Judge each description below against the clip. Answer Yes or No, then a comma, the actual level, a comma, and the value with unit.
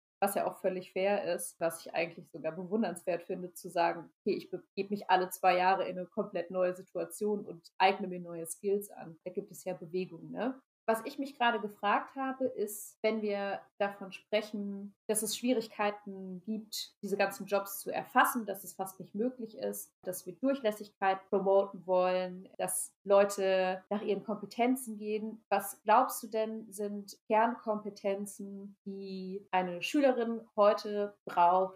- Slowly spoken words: No, average, 160 wpm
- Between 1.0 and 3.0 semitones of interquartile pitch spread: Yes, narrow, 2.4 semitones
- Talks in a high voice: Yes, high, 200 Hz